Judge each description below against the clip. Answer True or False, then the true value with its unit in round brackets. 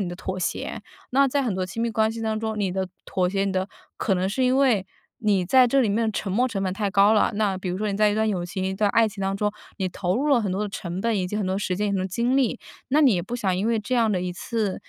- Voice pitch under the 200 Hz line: False (205 Hz)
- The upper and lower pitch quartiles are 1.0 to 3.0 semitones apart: False (3.4 semitones)